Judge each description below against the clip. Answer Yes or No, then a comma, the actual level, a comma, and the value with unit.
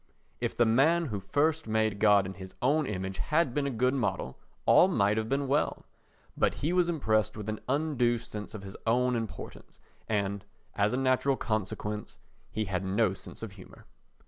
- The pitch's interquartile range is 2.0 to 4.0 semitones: No, average, 5.1 semitones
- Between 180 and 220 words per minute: Yes, average, 185 wpm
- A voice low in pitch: Yes, low, 110 Hz